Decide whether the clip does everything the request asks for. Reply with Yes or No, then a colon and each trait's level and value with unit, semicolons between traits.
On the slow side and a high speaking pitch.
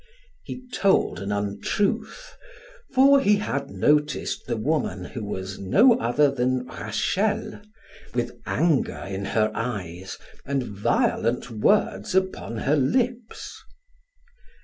No: slow, 110 wpm; low, 135 Hz